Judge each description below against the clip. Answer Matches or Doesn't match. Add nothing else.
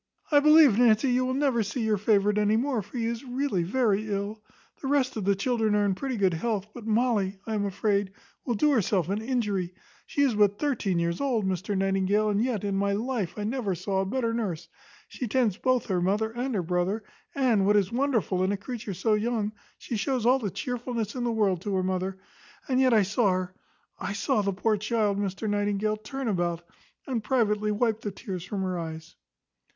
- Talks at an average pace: Doesn't match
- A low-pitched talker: Doesn't match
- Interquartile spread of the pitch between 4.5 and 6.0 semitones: Doesn't match